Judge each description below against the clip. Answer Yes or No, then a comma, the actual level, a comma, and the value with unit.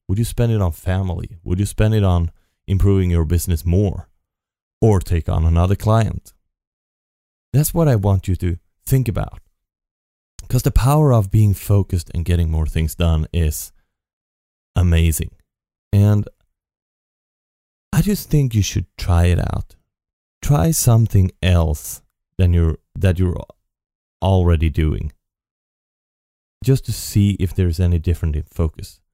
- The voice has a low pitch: Yes, very low, 90 Hz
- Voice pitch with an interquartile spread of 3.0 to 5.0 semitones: Yes, average, 3.8 semitones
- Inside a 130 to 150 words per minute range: Yes, average, 140 wpm